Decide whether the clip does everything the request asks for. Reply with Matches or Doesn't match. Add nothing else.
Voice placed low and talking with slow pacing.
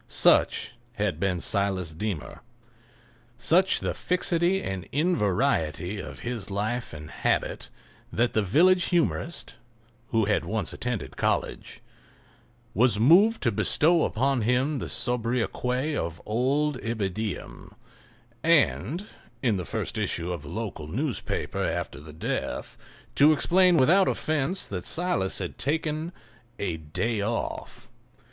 Matches